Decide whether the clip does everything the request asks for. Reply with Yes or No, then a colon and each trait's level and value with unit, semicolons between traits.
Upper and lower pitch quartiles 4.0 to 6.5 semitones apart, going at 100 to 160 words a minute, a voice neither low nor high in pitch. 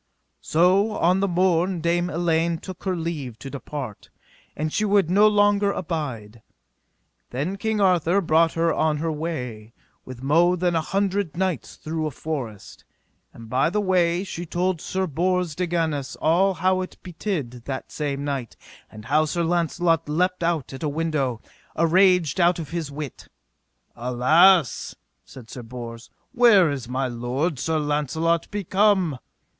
Yes: average, 4.4 semitones; average, 155 wpm; medium, 165 Hz